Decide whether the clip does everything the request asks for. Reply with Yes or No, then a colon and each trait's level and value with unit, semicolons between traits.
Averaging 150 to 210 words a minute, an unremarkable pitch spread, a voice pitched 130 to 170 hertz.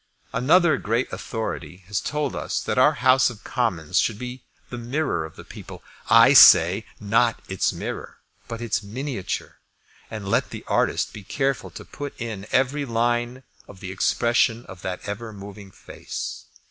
No: average, 160 wpm; average, 4.0 semitones; low, 115 Hz